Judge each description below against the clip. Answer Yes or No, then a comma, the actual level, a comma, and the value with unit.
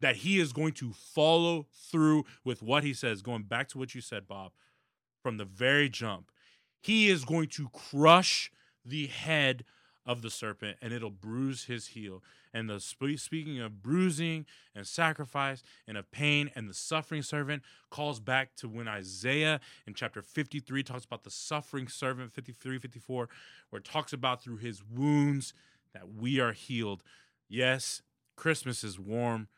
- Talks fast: No, average, 165 wpm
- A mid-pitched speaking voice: No, low, 130 Hz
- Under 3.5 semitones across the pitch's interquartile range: No, average, 4.3 semitones